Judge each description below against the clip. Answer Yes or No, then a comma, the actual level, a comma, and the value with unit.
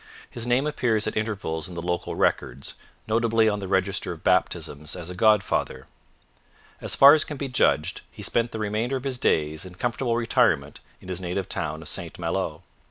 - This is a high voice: No, low, 105 Hz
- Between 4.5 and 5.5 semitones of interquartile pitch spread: Yes, average, 5.2 semitones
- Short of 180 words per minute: No, average, 190 wpm